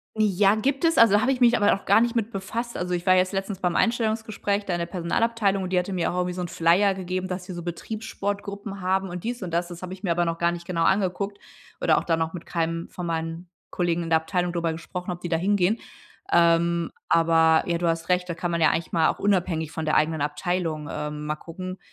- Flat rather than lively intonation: No, average, 3.0 semitones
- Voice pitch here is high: No, medium, 180 Hz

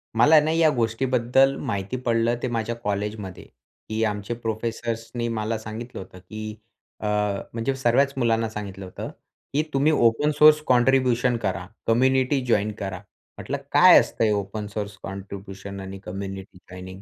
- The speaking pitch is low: Yes, low, 115 Hz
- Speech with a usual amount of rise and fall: Yes, average, 3.6 semitones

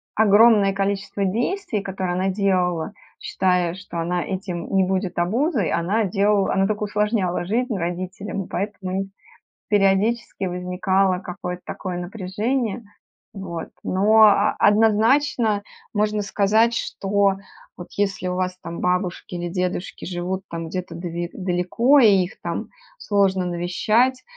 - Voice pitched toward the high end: Yes, high, 195 Hz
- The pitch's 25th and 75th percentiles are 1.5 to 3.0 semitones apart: Yes, narrow, 2.6 semitones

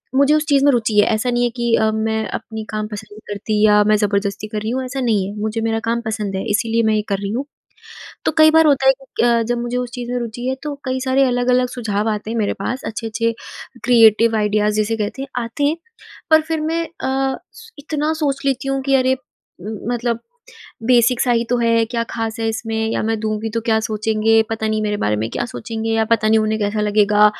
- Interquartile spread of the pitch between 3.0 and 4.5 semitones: No, narrow, 2.6 semitones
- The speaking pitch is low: No, high, 225 Hz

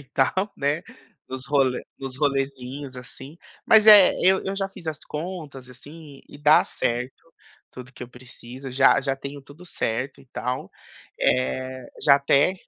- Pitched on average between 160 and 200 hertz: No, medium, 140 Hz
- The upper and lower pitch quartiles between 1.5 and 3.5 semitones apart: Yes, average, 2.9 semitones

